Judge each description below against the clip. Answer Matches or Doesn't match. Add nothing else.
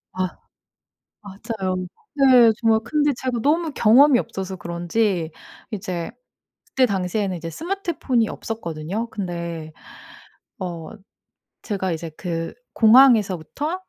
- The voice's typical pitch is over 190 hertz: Matches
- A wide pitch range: Matches